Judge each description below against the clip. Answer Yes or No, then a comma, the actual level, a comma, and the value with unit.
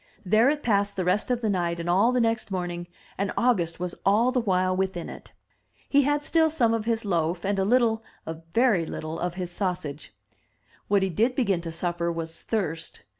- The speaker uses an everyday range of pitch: Yes, average, 4.8 semitones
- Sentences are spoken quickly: Yes, fast, 210 wpm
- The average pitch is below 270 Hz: Yes, high, 190 Hz